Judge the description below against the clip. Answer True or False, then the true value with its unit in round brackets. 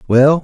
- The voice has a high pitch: False (140 Hz)